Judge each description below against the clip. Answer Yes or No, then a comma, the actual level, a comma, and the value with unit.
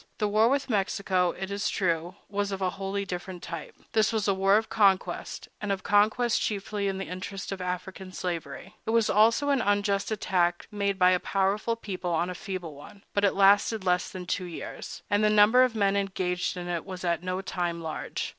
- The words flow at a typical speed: No, fast, 210 wpm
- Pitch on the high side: Yes, high, 195 Hz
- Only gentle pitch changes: Yes, narrow, 2.3 semitones